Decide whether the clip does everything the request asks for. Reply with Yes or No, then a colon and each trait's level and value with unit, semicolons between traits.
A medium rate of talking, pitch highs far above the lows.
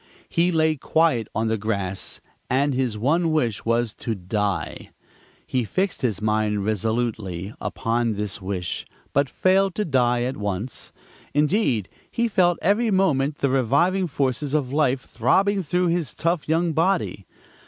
Yes: average, 145 wpm; wide, 7.3 semitones